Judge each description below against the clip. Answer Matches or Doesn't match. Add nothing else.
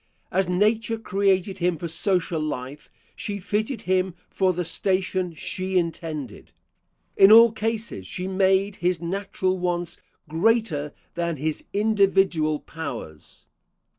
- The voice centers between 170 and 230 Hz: Matches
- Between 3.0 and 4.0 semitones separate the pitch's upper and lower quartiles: Matches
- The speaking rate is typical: Doesn't match